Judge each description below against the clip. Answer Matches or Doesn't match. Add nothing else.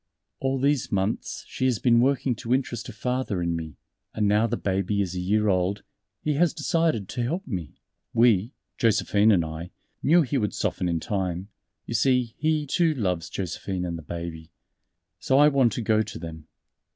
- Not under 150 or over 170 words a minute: Doesn't match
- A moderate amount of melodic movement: Doesn't match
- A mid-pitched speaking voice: Doesn't match